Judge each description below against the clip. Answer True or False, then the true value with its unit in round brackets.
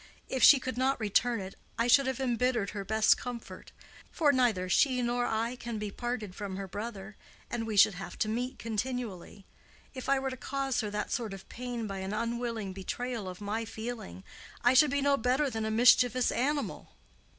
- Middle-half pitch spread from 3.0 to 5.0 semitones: True (3.3 semitones)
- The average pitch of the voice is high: True (235 Hz)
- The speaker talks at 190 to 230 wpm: True (195 wpm)